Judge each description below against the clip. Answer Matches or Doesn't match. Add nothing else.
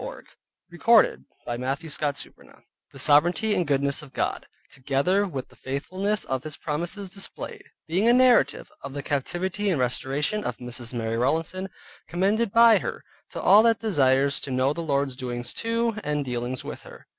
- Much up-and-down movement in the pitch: Matches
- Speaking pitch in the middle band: Matches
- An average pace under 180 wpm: Matches